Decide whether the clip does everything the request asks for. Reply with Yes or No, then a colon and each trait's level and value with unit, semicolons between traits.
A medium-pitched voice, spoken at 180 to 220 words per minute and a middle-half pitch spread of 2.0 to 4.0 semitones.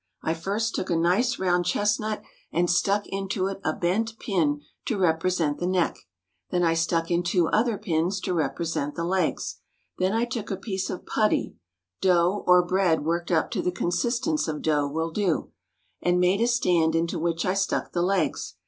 Yes: medium, 180 Hz; average, 185 wpm; average, 2.9 semitones